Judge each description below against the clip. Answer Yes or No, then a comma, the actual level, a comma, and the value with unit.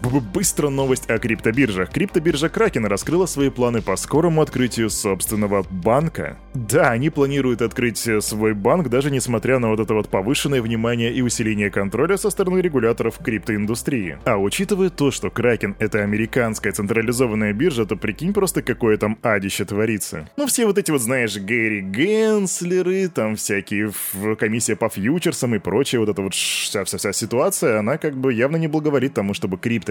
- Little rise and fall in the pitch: No, wide, 5.5 semitones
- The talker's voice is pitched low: Yes, low, 120 Hz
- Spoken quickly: Yes, fast, 165 wpm